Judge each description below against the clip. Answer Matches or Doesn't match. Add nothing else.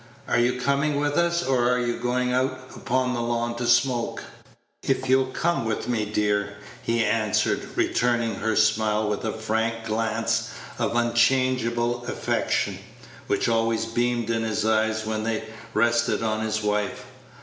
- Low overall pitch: Matches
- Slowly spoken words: Doesn't match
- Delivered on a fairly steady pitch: Matches